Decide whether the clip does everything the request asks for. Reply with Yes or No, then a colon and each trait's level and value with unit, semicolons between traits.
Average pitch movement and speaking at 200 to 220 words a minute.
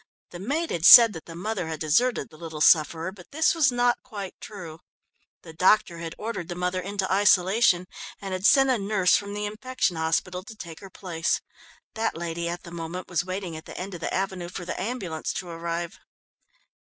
Yes: average, 3.6 semitones; fast, 205 wpm